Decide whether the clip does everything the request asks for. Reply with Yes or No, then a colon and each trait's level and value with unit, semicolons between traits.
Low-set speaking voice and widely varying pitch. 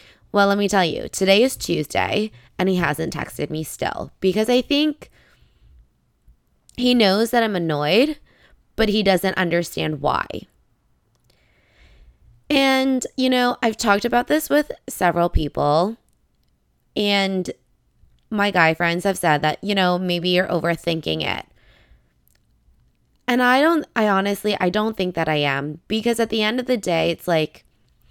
No: medium, 185 Hz; wide, 6.6 semitones